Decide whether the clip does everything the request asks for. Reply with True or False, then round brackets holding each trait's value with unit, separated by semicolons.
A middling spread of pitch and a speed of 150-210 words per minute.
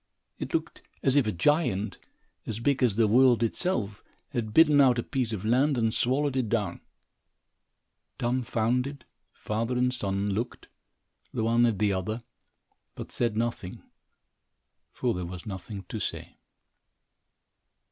False (3.3 semitones; 140 wpm)